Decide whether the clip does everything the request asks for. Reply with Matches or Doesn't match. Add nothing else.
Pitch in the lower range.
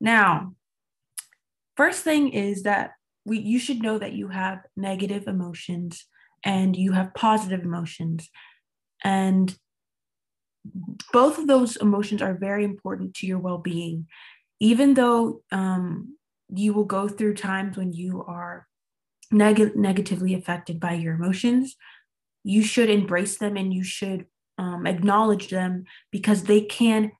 Doesn't match